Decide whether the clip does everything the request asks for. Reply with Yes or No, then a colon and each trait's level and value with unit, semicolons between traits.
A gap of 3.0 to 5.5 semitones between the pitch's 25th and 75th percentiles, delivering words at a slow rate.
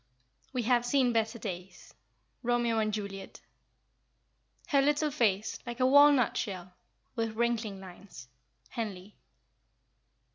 Yes: average, 3.8 semitones; slow, 110 wpm